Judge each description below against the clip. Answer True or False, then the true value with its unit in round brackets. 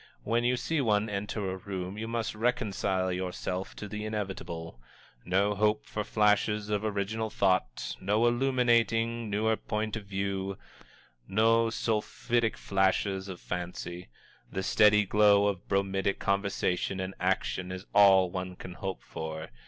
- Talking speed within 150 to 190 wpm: False (140 wpm)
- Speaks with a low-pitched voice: True (100 Hz)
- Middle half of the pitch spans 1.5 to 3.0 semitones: True (2.5 semitones)